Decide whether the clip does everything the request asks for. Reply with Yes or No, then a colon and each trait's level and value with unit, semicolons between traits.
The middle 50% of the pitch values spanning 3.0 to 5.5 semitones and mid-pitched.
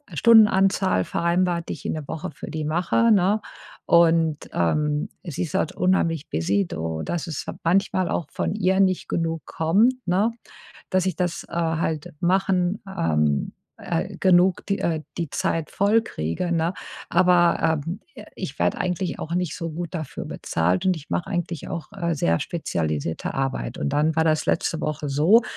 Yes: average, 3.4 semitones; medium, 170 Hz